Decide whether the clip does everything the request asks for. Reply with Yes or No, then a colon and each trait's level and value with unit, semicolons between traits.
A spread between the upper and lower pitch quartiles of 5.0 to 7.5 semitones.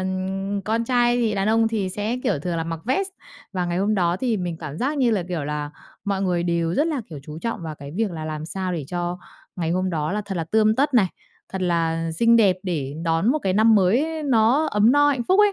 Yes: average, 5.3 semitones